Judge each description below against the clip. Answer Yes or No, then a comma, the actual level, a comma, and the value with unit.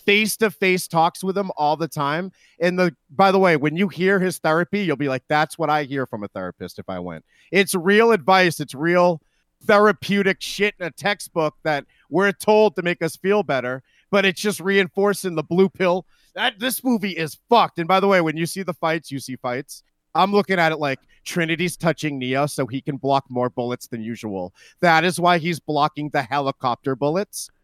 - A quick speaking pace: Yes, fast, 215 wpm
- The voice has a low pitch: No, medium, 170 Hz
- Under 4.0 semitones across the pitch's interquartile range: No, average, 5.1 semitones